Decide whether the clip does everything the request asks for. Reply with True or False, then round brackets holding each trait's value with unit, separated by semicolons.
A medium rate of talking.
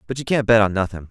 False (325 wpm)